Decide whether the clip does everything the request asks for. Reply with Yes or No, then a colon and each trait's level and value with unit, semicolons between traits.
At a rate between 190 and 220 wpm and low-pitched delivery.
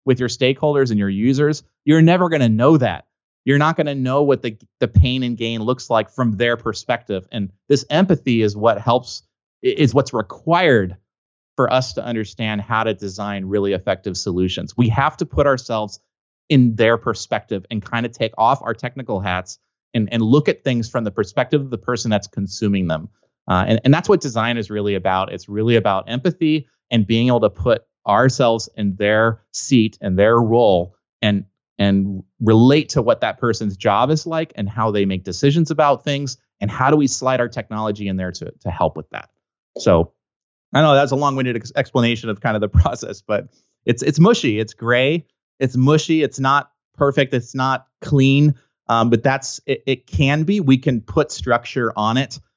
Yes: average, 200 wpm; low, 120 Hz